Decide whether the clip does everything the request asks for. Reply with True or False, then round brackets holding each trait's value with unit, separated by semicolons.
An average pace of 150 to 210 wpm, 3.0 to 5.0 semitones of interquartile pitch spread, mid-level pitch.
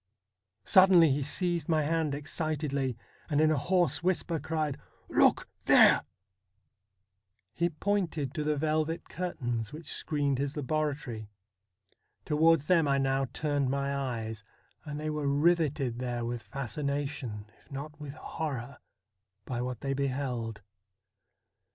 False (135 wpm; 3.5 semitones; 145 Hz)